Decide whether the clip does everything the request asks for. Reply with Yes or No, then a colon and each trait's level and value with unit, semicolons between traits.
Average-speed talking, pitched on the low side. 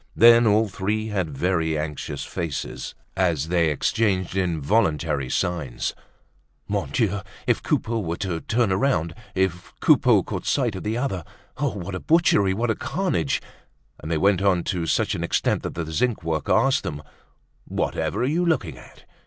Yes: average, 160 wpm; very low, 95 Hz